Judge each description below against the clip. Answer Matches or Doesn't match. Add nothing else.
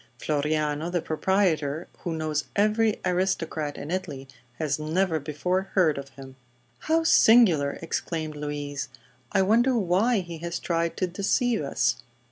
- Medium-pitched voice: Matches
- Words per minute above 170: Doesn't match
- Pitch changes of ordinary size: Matches